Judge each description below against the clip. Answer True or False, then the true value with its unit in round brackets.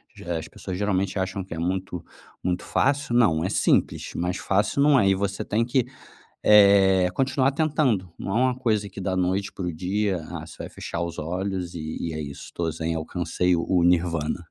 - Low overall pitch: True (95 Hz)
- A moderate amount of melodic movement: True (3.2 semitones)